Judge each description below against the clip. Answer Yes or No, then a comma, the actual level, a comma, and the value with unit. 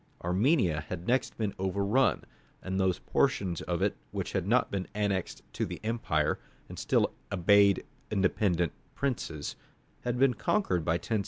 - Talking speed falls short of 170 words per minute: Yes, average, 150 wpm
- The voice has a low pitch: Yes, low, 100 Hz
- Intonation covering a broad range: No, average, 4.6 semitones